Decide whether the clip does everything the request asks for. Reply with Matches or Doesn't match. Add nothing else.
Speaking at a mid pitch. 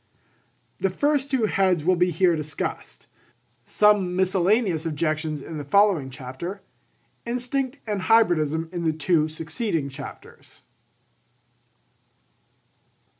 Matches